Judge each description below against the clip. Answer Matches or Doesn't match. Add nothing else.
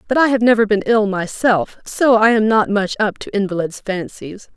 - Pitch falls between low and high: Doesn't match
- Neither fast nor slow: Doesn't match